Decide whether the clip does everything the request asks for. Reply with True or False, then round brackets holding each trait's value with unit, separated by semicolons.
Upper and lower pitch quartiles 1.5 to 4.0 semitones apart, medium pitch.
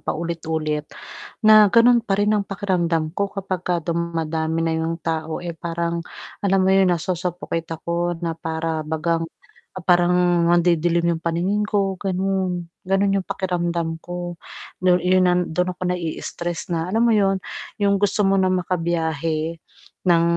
True (2.5 semitones; 175 Hz)